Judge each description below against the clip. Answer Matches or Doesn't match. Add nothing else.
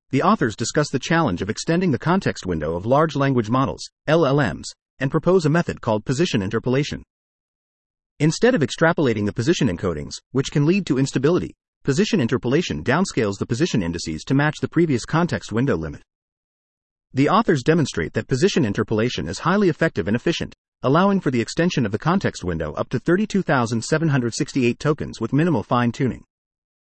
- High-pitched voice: Doesn't match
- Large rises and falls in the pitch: Matches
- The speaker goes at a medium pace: Matches